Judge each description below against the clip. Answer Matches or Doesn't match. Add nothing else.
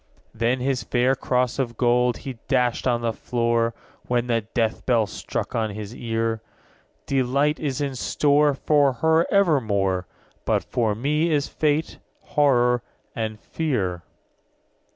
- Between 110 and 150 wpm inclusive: Matches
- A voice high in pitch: Doesn't match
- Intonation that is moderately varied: Matches